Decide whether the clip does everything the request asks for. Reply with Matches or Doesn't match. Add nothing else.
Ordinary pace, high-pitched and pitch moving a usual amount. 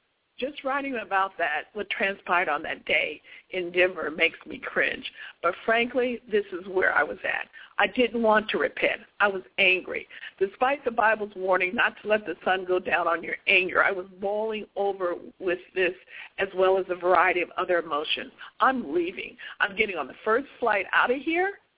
Matches